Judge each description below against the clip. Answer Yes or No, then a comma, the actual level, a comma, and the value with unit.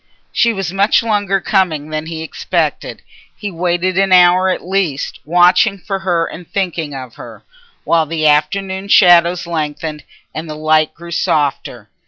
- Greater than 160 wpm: No, average, 155 wpm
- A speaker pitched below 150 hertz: No, medium, 175 Hz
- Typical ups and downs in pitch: Yes, average, 3.5 semitones